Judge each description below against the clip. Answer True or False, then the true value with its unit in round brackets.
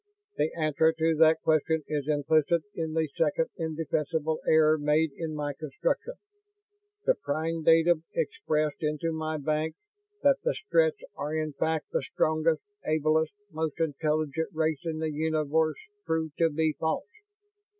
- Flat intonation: True (1.0 semitones)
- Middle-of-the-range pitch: True (155 Hz)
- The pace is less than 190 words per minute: True (140 wpm)